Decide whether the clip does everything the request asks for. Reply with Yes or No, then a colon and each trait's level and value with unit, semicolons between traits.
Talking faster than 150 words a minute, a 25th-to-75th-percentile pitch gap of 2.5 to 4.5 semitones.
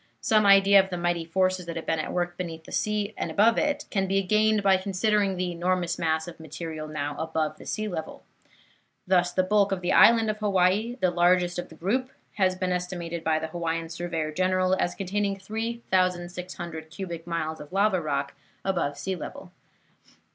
Yes: average, 190 wpm; average, 2.8 semitones